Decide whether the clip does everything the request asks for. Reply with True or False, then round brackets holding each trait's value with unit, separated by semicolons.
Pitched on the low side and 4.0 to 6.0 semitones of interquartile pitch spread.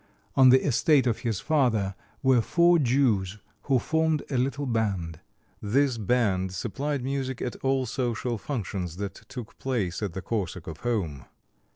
True (120 Hz; 5.3 semitones)